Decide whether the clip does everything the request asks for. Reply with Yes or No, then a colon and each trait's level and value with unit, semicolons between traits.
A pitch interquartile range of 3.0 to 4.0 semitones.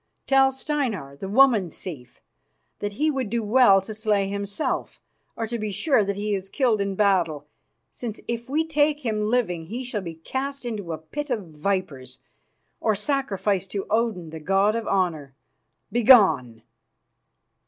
No: average, 4.8 semitones